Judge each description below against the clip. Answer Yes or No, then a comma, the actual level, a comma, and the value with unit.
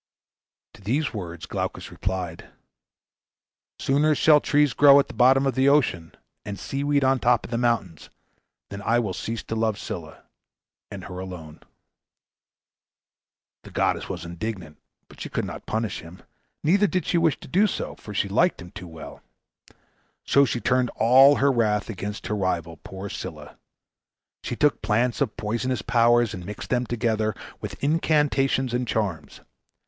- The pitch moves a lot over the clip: Yes, wide, 5.7 semitones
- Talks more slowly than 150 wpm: No, average, 165 wpm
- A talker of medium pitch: No, low, 115 Hz